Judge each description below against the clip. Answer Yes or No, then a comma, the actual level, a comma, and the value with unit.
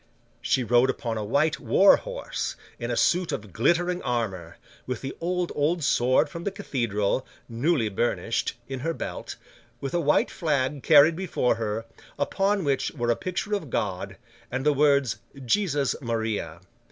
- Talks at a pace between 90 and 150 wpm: No, average, 160 wpm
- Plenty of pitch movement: Yes, wide, 6.3 semitones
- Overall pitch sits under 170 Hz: Yes, low, 135 Hz